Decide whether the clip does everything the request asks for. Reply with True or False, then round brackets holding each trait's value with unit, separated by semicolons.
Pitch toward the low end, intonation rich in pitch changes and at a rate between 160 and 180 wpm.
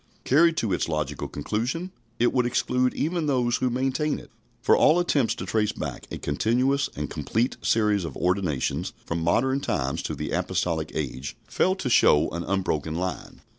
True (110 Hz; 8.3 semitones; 170 wpm)